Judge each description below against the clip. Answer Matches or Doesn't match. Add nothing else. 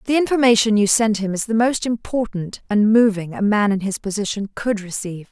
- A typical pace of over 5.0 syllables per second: Matches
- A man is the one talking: Doesn't match